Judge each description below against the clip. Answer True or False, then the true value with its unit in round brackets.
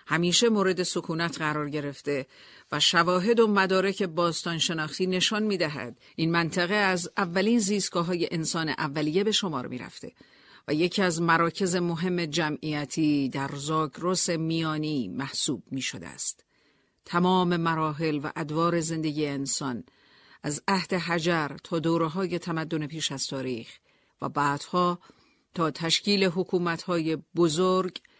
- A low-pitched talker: False (170 Hz)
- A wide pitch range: False (3.1 semitones)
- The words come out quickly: False (130 wpm)